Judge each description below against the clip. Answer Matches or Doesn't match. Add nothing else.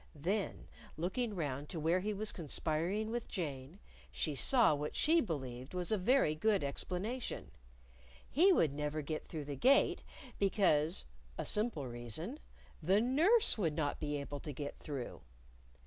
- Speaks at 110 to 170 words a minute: Matches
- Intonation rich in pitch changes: Matches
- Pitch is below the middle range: Doesn't match